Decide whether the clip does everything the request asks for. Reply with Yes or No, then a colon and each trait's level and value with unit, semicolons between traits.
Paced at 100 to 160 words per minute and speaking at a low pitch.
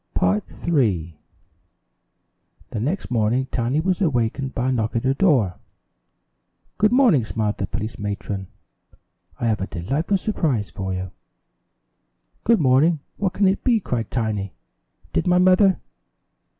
Yes: average, 140 wpm; low, 125 Hz